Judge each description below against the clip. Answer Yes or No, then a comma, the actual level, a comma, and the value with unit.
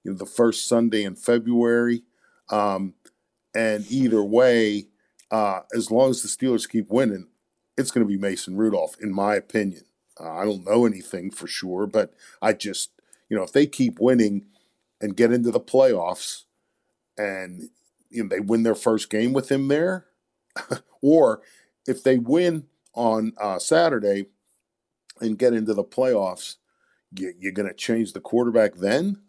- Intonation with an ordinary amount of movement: Yes, average, 3.2 semitones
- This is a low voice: Yes, low, 110 Hz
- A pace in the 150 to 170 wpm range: Yes, average, 160 wpm